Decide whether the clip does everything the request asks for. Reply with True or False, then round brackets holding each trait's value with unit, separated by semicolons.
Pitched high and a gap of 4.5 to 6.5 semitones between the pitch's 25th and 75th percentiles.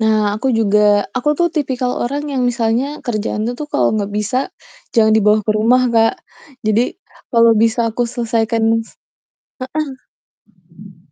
False (230 Hz; 2.7 semitones)